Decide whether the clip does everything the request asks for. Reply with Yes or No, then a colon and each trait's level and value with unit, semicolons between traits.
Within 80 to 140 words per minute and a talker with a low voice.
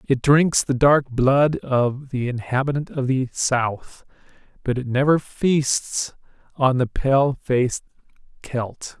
Yes: slow, 135 wpm; low, 130 Hz